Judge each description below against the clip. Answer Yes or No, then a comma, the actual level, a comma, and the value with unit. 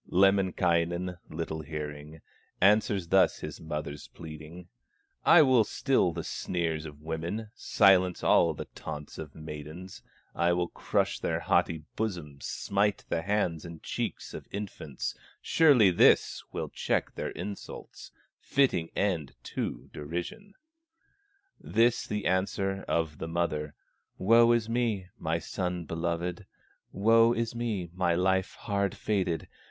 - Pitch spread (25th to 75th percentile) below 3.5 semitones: No, average, 4.1 semitones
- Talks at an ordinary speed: No, slow, 125 wpm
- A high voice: No, very low, 90 Hz